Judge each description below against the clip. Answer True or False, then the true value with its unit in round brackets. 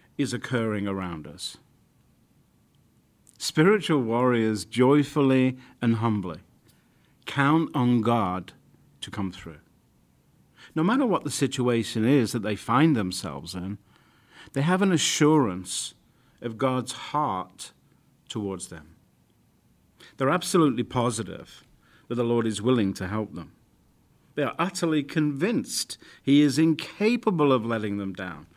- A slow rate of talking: True (120 wpm)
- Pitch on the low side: True (120 Hz)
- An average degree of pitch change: False (6.2 semitones)